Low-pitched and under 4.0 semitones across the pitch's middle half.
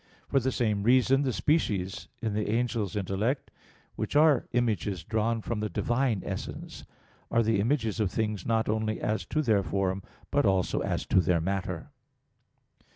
Yes: low, 110 Hz; average, 3.6 semitones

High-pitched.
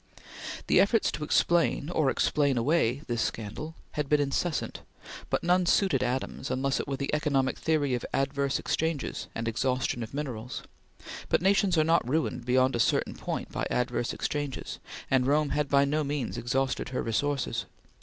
No: medium, 140 Hz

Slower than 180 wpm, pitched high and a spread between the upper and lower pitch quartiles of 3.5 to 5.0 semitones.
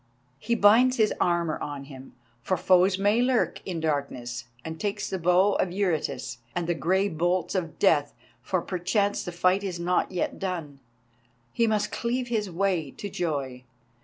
No: average, 165 wpm; medium, 180 Hz; average, 4.0 semitones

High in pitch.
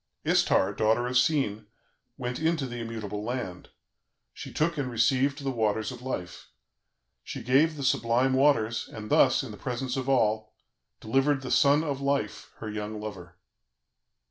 No: low, 125 Hz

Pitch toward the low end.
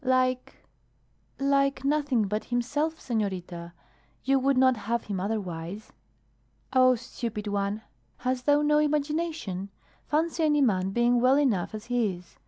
No: high, 245 Hz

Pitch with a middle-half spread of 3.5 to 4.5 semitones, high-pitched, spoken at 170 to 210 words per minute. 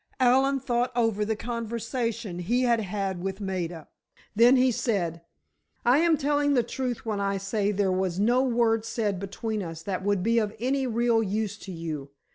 Yes: average, 3.9 semitones; high, 220 Hz; average, 180 wpm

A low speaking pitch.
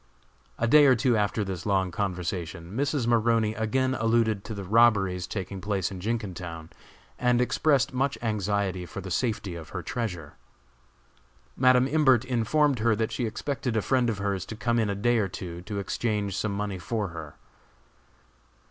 Yes: low, 105 Hz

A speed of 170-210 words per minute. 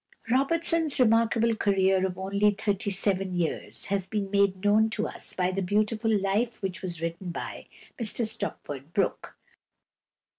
No: average, 145 wpm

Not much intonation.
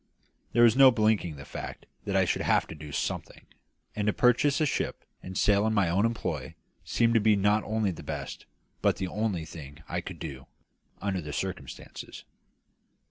No: average, 4.9 semitones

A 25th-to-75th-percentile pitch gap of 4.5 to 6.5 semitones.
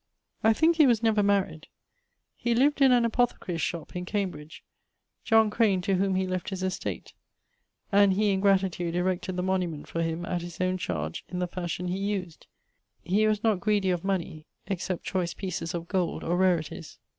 No: average, 2.8 semitones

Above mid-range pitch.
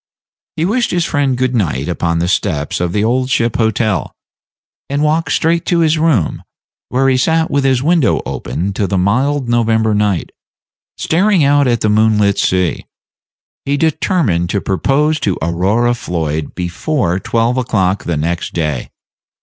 No: low, 115 Hz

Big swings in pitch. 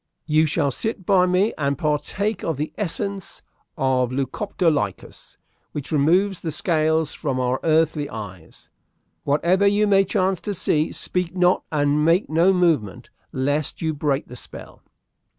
No: average, 4.3 semitones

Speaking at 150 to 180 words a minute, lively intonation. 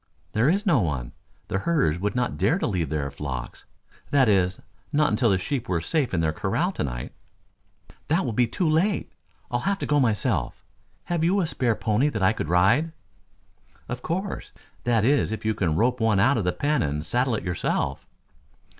No: average, 200 wpm; wide, 8.2 semitones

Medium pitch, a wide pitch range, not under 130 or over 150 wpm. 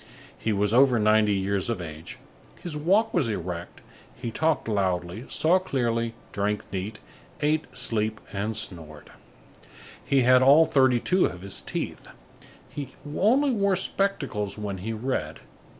No: low, 115 Hz; wide, 6.8 semitones; average, 140 wpm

